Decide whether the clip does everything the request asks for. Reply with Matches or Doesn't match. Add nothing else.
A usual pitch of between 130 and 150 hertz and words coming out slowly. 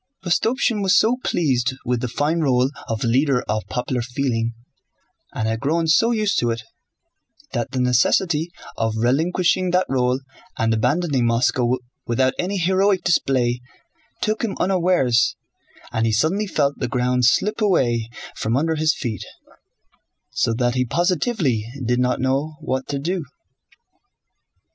Doesn't match